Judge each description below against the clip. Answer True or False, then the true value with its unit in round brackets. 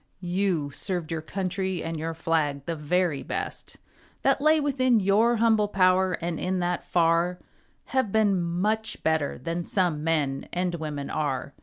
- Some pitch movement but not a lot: True (3.7 semitones)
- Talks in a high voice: False (175 Hz)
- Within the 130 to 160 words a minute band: True (155 wpm)